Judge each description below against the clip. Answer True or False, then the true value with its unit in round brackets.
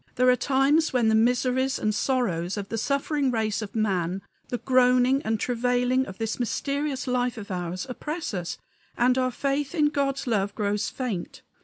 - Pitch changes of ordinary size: True (3.8 semitones)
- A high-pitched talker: True (250 Hz)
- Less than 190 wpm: True (175 wpm)